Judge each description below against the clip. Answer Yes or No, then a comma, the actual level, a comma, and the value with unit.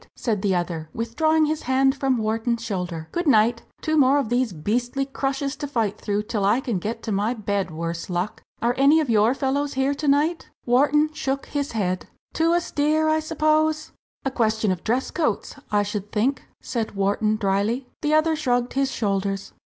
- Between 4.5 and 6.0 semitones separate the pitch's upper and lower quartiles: Yes, wide, 5.6 semitones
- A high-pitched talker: Yes, high, 245 Hz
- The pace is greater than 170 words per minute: Yes, average, 185 wpm